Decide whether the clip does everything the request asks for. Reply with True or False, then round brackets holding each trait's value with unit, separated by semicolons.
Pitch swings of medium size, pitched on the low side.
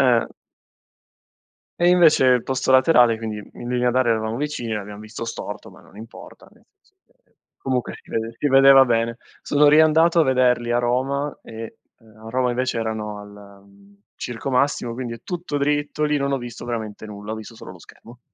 True (3.5 semitones; 120 Hz)